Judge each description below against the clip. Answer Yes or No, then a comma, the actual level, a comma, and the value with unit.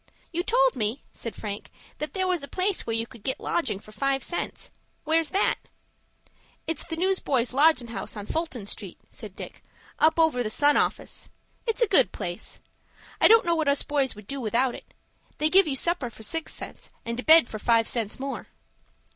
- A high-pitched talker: Yes, very high, 275 Hz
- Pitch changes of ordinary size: No, wide, 6.0 semitones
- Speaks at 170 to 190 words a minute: No, average, 200 wpm